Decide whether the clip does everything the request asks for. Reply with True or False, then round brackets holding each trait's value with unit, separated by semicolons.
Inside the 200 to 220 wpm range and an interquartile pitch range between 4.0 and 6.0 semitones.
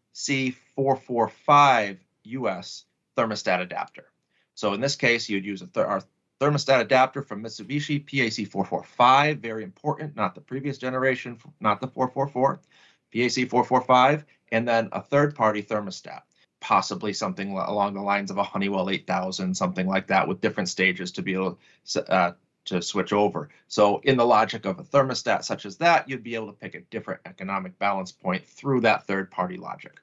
False (165 wpm; 5.1 semitones)